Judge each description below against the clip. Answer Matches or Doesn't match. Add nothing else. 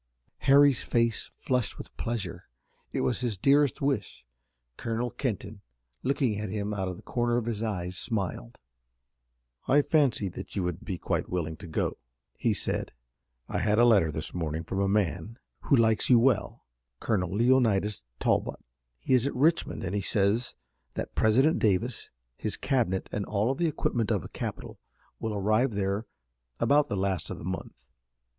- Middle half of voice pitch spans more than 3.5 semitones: Matches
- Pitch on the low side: Matches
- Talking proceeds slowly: Doesn't match